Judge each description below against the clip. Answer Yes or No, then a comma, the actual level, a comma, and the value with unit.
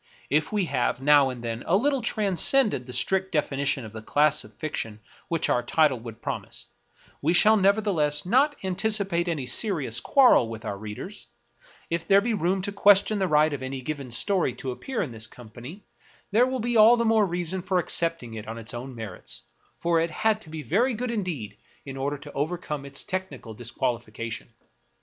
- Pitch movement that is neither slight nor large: No, wide, 7.9 semitones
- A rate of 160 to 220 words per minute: Yes, average, 200 wpm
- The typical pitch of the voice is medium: Yes, medium, 160 Hz